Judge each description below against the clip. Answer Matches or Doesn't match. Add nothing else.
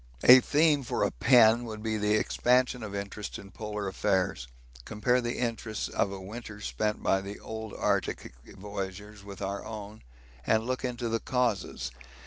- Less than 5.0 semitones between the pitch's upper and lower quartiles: Matches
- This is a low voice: Matches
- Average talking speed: Matches